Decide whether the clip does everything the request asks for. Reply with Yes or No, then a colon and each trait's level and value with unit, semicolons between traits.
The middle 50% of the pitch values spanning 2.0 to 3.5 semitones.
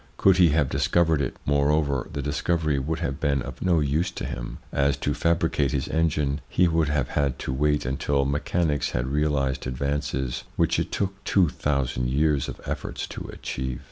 Yes: average, 2.7 semitones